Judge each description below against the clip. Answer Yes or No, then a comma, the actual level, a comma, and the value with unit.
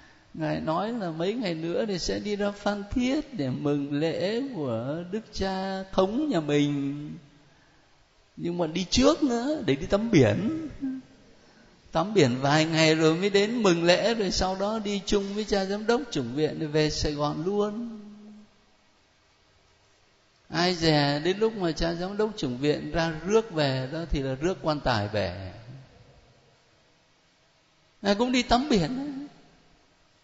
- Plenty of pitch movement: Yes, wide, 6.3 semitones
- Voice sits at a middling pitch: Yes, medium, 170 Hz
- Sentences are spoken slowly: Yes, slow, 160 wpm